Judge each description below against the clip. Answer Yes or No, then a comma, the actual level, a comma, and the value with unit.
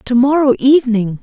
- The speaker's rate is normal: Yes, average, 145 wpm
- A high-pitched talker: Yes, very high, 250 Hz